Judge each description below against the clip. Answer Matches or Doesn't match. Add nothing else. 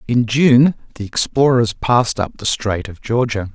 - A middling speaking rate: Matches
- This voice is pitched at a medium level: Doesn't match